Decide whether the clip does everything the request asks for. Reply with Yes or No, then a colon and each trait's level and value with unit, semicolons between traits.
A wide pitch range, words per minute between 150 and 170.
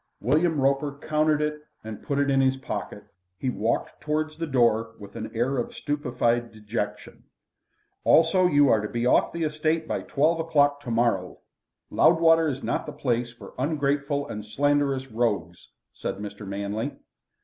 No: average, 4.8 semitones; average, 160 wpm